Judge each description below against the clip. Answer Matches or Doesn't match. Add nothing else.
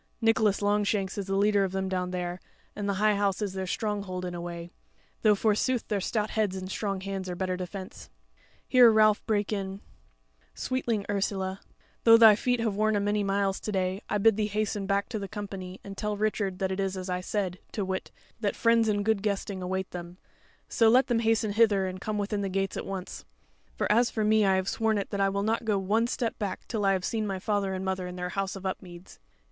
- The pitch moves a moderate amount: Doesn't match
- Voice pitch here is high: Matches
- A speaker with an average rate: Doesn't match